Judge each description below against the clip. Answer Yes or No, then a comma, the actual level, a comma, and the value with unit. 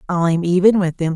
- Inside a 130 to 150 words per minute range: No, fast, 205 wpm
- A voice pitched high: No, medium, 175 Hz